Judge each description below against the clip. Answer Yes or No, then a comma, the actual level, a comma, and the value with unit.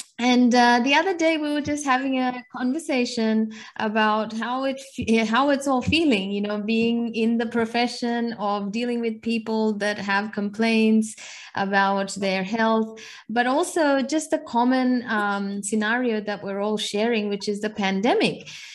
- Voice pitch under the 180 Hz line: No, high, 230 Hz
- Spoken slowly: No, average, 155 wpm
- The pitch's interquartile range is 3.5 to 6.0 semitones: No, average, 3.1 semitones